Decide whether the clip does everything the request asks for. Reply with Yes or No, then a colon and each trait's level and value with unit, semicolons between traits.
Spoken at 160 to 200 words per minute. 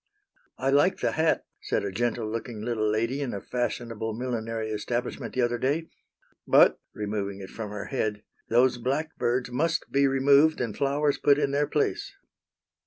Yes: average, 165 wpm